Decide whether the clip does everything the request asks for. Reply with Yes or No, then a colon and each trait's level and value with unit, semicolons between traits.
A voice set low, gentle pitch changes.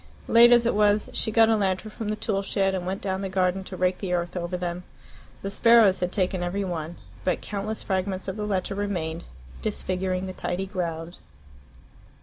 No: high, 190 Hz; narrow, 2.2 semitones